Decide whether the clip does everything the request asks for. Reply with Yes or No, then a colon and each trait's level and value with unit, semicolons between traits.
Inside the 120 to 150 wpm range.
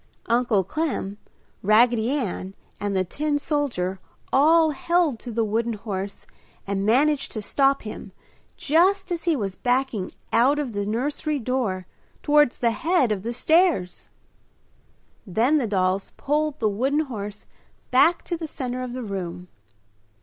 Yes: average, 145 wpm